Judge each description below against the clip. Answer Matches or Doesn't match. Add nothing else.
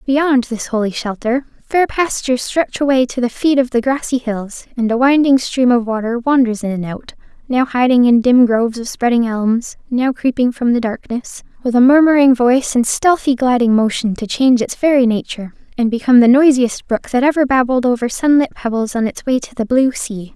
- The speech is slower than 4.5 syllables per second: Doesn't match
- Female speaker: Matches